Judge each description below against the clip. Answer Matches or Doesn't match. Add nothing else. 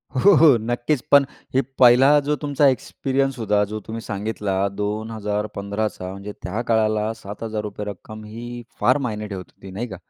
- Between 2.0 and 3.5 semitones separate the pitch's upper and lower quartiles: Matches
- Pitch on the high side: Doesn't match